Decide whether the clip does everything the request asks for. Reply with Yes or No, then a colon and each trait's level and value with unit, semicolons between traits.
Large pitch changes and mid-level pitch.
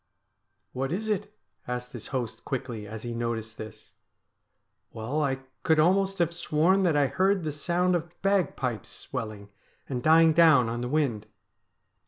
Yes: wide, 6.3 semitones; medium, 145 Hz